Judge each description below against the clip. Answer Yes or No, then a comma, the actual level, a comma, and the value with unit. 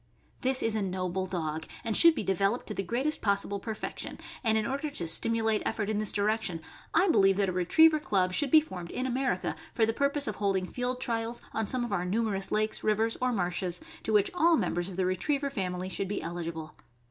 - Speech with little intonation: No, average, 4.9 semitones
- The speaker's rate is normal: No, fast, 215 wpm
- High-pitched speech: Yes, high, 210 Hz